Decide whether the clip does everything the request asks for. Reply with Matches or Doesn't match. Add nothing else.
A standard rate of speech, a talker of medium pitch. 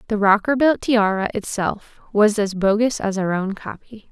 Doesn't match